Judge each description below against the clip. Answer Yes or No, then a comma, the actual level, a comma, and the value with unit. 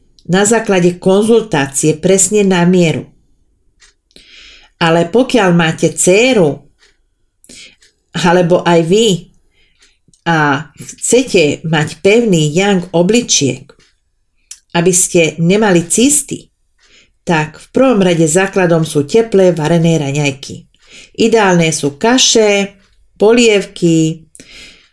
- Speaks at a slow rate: Yes, slow, 85 wpm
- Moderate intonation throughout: Yes, average, 3.7 semitones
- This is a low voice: No, medium, 180 Hz